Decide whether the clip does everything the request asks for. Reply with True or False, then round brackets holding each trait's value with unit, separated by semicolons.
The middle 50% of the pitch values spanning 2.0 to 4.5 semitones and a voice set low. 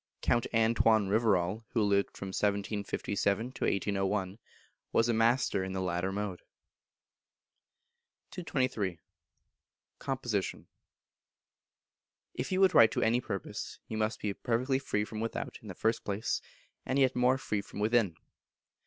True (3.2 semitones; 110 Hz)